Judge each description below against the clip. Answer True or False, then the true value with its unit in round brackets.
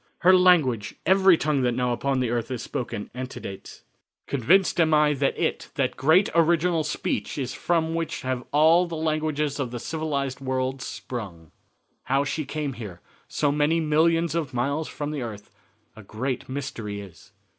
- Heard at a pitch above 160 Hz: False (140 Hz)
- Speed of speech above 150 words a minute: True (165 wpm)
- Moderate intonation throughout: True (4.2 semitones)